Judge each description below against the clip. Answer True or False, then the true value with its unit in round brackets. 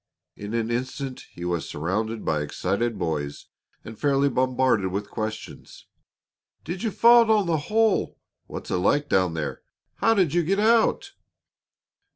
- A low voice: True (125 Hz)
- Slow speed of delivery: False (155 wpm)